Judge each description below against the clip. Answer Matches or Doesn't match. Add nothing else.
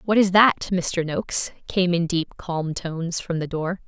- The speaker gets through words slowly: Doesn't match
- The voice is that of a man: Doesn't match